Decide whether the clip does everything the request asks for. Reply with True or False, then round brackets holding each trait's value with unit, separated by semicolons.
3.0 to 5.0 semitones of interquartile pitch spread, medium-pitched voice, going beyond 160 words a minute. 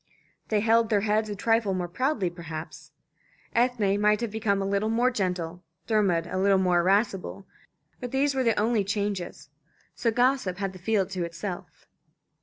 False (3.4 semitones; 205 Hz; 170 wpm)